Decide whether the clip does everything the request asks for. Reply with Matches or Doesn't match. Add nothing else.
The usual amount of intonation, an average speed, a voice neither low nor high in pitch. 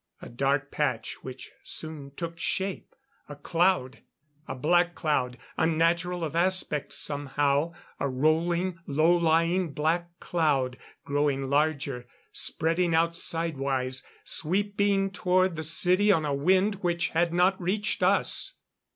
Doesn't match